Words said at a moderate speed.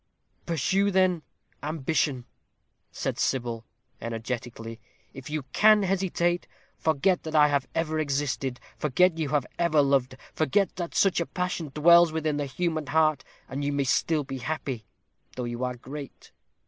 Yes: average, 150 wpm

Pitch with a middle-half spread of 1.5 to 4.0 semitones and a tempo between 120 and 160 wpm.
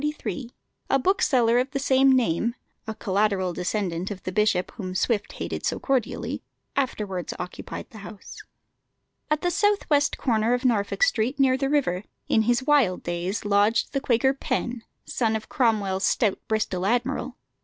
No: average, 4.8 semitones; average, 155 wpm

